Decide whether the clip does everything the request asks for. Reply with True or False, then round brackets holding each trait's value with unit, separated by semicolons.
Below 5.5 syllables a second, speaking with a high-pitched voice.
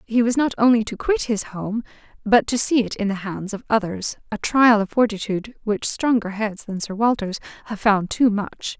True (5.0 syllables/s; 220 Hz)